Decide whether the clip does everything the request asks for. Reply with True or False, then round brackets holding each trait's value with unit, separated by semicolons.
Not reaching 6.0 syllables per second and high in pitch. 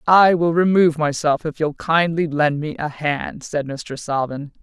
False (4.3 syllables/s; 155 Hz)